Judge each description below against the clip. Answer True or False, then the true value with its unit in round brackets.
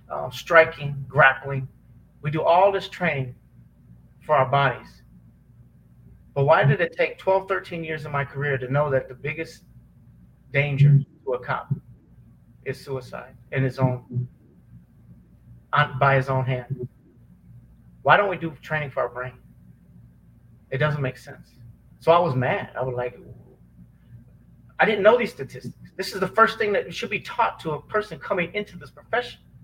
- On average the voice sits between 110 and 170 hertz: True (135 Hz)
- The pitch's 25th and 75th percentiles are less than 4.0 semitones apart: False (4.8 semitones)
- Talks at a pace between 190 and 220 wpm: False (165 wpm)